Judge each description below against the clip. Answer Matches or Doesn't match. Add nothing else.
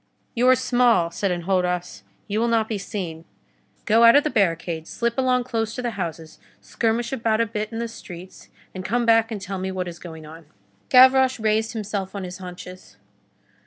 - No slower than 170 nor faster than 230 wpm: Matches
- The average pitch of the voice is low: Doesn't match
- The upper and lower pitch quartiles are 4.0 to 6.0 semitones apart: Matches